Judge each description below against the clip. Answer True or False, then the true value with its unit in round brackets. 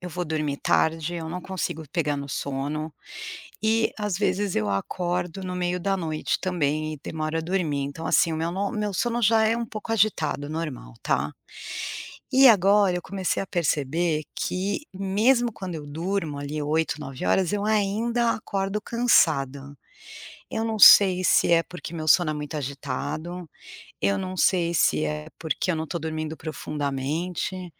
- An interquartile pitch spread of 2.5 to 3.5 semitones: False (4.3 semitones)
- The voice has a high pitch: False (170 Hz)